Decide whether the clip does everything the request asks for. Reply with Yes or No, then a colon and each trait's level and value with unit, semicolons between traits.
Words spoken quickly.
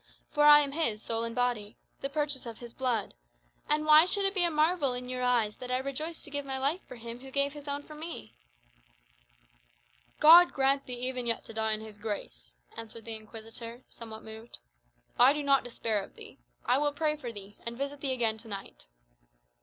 Yes: fast, 210 wpm